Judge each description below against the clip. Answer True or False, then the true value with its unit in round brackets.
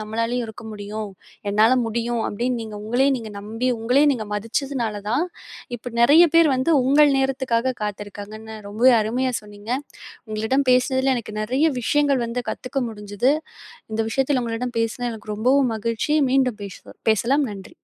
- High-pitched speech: True (235 Hz)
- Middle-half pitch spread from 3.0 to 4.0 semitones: True (3.3 semitones)